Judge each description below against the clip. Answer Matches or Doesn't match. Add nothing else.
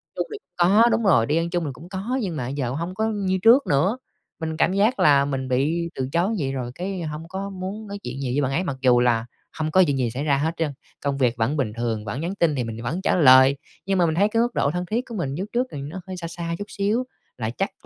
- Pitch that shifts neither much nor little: Doesn't match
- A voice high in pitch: Doesn't match